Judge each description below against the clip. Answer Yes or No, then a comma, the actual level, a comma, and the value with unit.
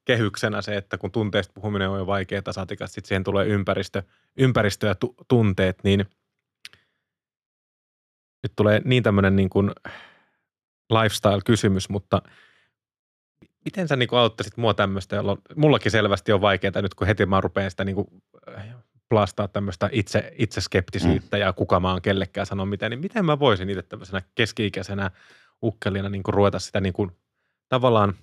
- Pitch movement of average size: No, narrow, 2.1 semitones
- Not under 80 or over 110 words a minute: No, average, 145 wpm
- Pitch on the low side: Yes, low, 100 Hz